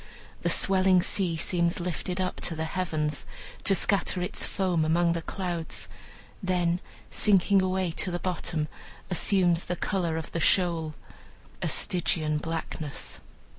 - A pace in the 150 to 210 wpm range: No, slow, 135 wpm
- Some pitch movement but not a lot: No, narrow, 2.3 semitones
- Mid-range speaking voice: Yes, medium, 175 Hz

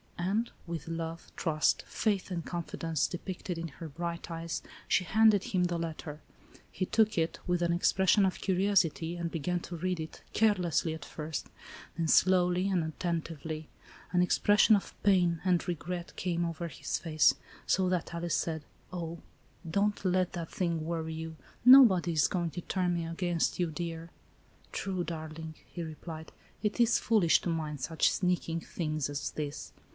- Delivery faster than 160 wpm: Yes, average, 170 wpm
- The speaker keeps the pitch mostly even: Yes, narrow, 2.1 semitones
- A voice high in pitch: No, medium, 170 Hz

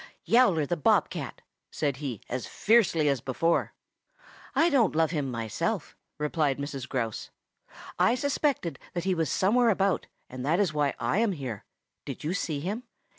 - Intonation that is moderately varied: No, wide, 6.2 semitones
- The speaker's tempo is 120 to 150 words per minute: No, average, 165 wpm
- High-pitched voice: No, medium, 160 Hz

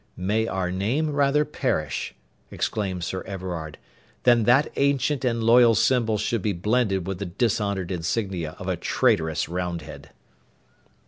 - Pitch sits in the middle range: No, low, 105 Hz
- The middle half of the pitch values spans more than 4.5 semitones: Yes, average, 5.1 semitones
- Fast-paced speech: No, slow, 135 wpm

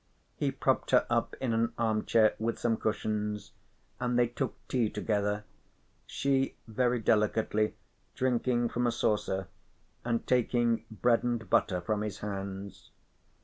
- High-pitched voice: No, low, 115 Hz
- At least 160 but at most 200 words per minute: No, slow, 135 wpm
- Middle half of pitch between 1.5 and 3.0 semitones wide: Yes, narrow, 2.4 semitones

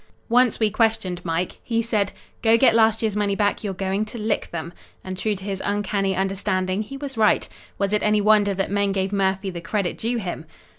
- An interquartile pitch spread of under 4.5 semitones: Yes, narrow, 2.4 semitones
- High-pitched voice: Yes, high, 205 Hz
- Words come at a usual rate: No, fast, 210 wpm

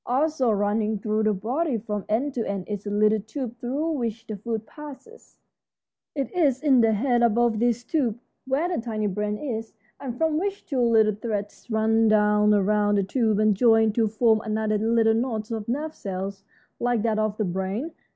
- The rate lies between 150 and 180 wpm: No, average, 190 wpm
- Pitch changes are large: No, average, 2.8 semitones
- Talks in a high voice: Yes, high, 225 Hz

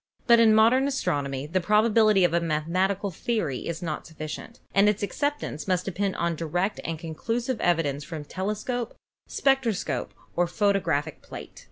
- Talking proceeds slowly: No, average, 155 wpm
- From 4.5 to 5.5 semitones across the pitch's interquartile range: Yes, average, 5.1 semitones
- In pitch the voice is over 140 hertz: Yes, medium, 185 Hz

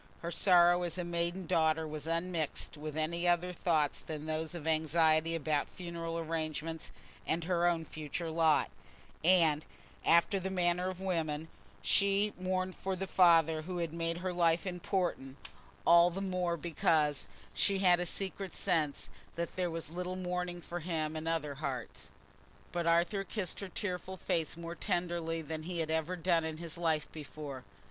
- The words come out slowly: No, average, 165 wpm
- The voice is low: No, medium, 170 Hz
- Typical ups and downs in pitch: No, narrow, 2.1 semitones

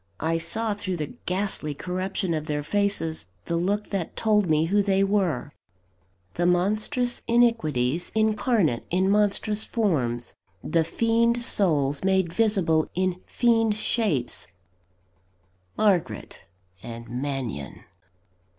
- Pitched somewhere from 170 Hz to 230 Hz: Yes, medium, 185 Hz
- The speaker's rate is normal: No, slow, 115 wpm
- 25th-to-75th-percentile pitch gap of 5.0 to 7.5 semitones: Yes, average, 5.3 semitones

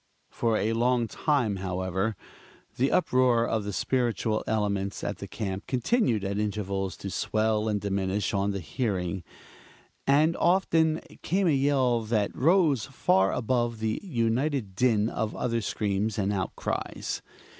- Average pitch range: Yes, average, 4.2 semitones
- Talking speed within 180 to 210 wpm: No, average, 140 wpm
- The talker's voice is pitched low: Yes, low, 110 Hz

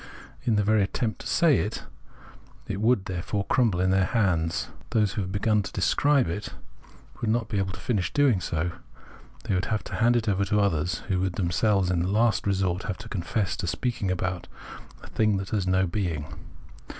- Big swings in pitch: No, average, 3.2 semitones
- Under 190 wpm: No, average, 200 wpm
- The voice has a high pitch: No, low, 100 Hz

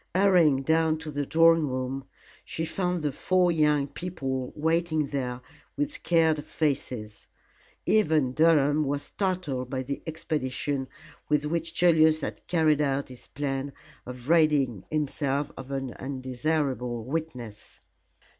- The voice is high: No, medium, 145 Hz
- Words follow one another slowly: Yes, slow, 125 wpm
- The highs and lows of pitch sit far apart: No, average, 3.4 semitones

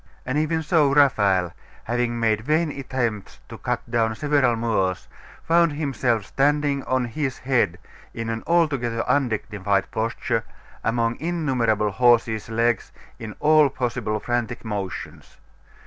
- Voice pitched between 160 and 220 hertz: No, low, 120 Hz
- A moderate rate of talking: No, slow, 125 wpm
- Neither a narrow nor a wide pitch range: Yes, average, 4.3 semitones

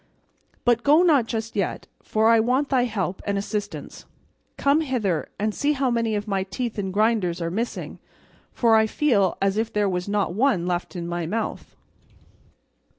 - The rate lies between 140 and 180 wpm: Yes, average, 175 wpm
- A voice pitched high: Yes, high, 215 Hz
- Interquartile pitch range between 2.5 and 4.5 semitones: Yes, average, 3.8 semitones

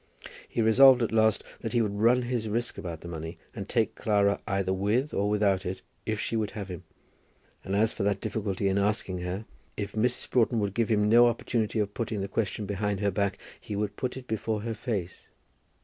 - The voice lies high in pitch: No, low, 105 Hz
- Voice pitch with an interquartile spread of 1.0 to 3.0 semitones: Yes, narrow, 2.4 semitones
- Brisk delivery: Yes, fast, 210 wpm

